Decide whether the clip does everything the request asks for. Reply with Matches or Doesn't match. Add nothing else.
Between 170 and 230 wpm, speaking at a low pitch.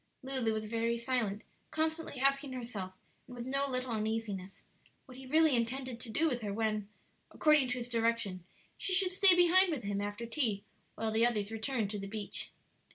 Doesn't match